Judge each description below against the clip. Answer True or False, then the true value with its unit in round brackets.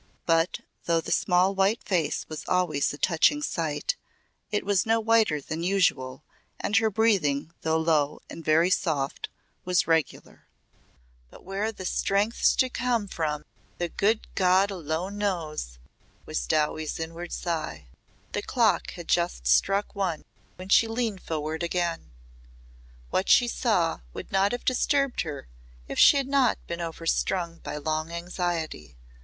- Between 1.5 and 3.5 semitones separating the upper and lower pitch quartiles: False (4.3 semitones)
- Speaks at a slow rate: False (145 wpm)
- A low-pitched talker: False (175 Hz)